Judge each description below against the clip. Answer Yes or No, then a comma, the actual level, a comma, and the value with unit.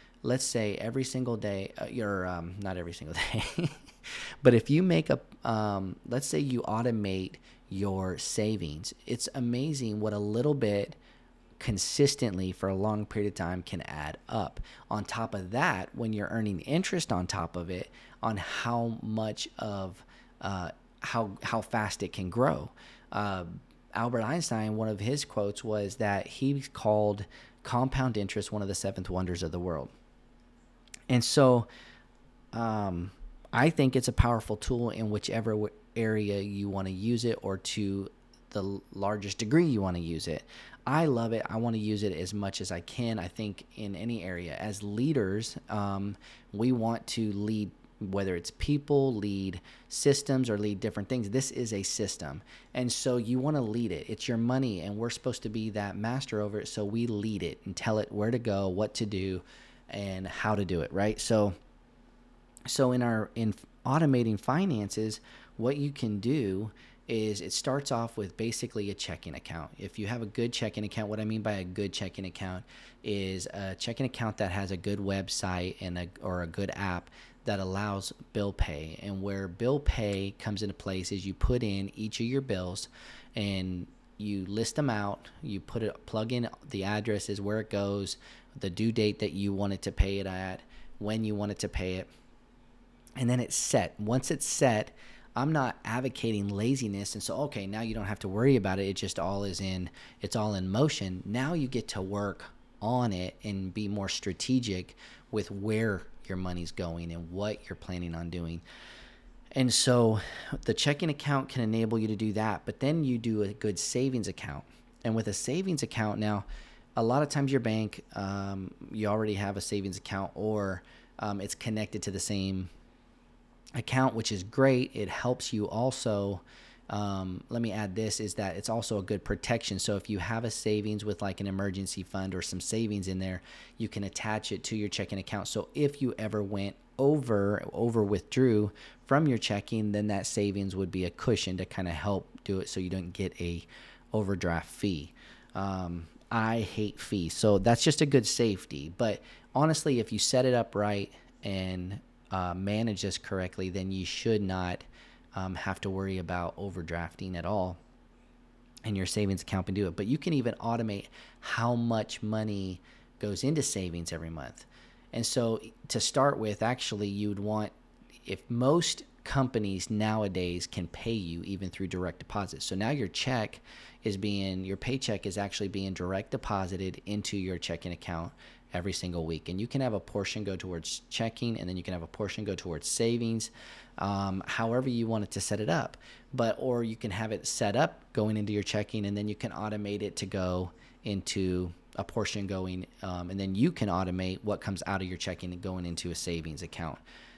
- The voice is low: Yes, low, 105 Hz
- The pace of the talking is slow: No, average, 190 wpm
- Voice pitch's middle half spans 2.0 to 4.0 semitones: Yes, average, 3.3 semitones